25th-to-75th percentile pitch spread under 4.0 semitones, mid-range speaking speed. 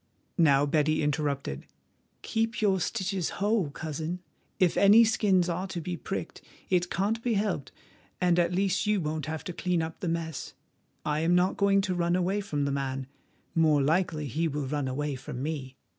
No: average, 4.3 semitones; average, 180 wpm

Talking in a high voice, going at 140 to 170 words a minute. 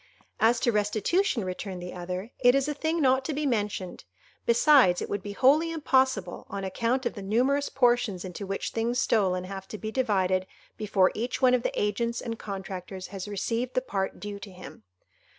No: high, 215 Hz; average, 190 wpm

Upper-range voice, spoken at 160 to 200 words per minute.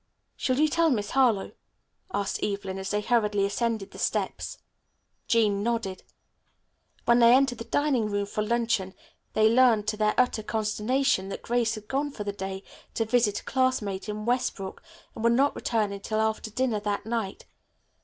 Yes: high, 220 Hz; average, 170 wpm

